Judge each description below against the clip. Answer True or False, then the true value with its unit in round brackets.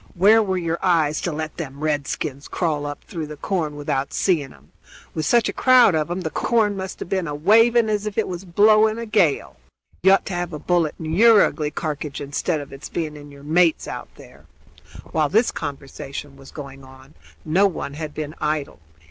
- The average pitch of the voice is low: False (160 Hz)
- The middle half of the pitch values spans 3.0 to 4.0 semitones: False (4.7 semitones)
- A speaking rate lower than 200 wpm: False (205 wpm)